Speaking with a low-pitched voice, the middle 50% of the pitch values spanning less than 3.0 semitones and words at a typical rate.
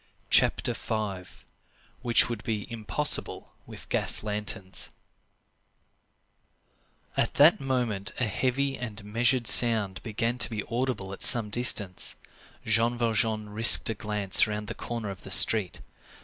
No: low, 110 Hz; narrow, 2.6 semitones; slow, 125 wpm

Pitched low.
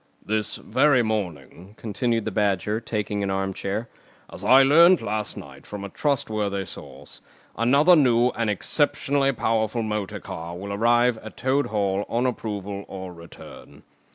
Yes: low, 110 Hz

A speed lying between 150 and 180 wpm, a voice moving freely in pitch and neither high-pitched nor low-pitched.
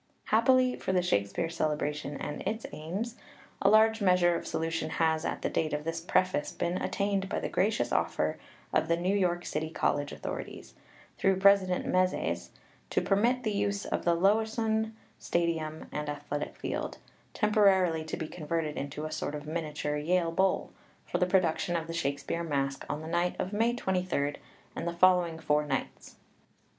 No: average, 175 wpm; average, 4.1 semitones; medium, 170 Hz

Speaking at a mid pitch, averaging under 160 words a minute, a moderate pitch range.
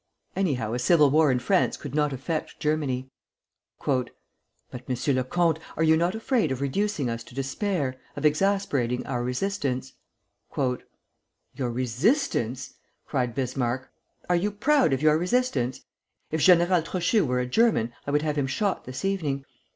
No: medium, 145 Hz; average, 150 wpm; wide, 5.7 semitones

